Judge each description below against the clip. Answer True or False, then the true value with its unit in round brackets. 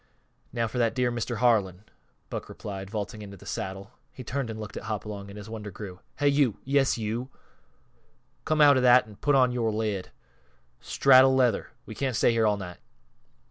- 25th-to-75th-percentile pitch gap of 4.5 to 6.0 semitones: False (3.6 semitones)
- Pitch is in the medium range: False (110 Hz)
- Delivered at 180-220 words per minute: True (190 wpm)